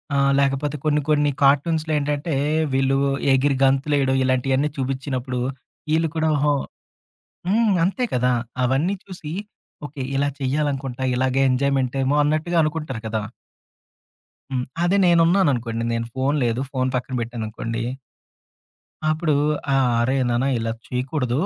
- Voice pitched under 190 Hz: Yes, low, 135 Hz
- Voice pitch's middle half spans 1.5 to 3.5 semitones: Yes, average, 2.9 semitones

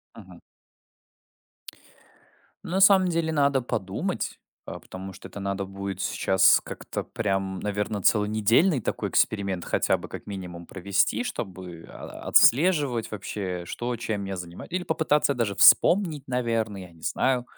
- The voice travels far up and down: Yes, wide, 5.7 semitones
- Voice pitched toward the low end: Yes, low, 105 Hz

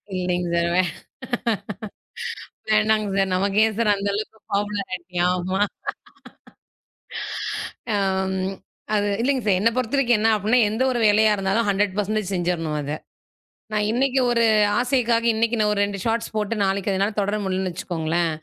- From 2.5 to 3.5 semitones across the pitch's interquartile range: Yes, average, 2.8 semitones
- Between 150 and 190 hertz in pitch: No, high, 205 Hz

